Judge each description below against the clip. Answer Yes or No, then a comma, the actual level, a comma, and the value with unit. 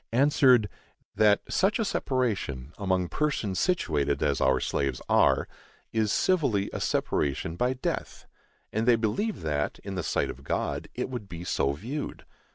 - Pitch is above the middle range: No, low, 105 Hz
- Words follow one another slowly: No, average, 155 wpm